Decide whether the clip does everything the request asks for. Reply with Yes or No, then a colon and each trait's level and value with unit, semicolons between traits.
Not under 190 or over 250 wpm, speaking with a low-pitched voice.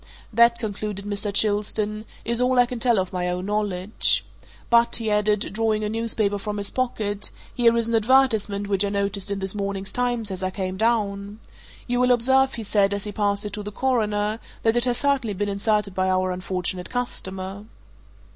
No: average, 195 wpm; high, 210 Hz